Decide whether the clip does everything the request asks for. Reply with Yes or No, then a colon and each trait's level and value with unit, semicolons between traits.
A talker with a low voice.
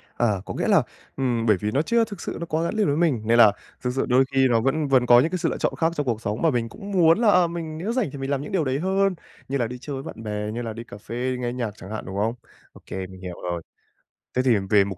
Yes: low, 130 Hz